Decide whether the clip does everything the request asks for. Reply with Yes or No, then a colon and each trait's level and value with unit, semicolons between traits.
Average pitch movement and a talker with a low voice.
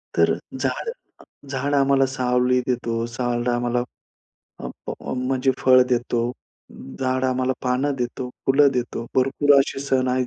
No: narrow, 1.4 semitones; low, 130 Hz